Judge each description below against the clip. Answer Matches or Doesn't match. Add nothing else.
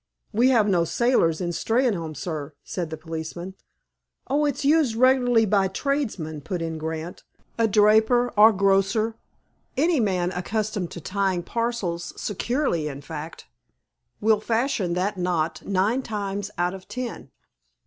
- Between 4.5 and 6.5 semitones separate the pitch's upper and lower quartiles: Matches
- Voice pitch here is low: Doesn't match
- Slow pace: Matches